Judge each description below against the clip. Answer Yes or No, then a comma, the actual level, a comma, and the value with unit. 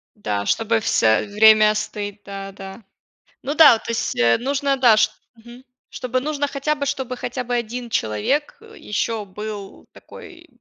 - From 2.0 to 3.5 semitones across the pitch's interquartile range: No, average, 4.7 semitones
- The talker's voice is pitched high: Yes, high, 230 Hz